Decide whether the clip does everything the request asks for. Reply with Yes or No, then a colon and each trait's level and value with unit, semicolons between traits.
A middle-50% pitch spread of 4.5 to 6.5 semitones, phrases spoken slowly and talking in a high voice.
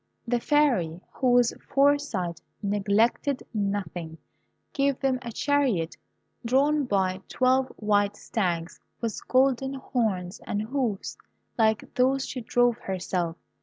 Yes: average, 5.2 semitones; slow, 110 wpm; high, 230 Hz